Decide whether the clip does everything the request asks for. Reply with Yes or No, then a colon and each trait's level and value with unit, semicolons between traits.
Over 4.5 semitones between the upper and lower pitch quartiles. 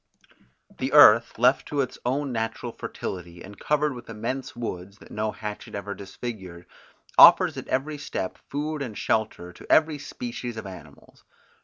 Yes: average, 5.2 semitones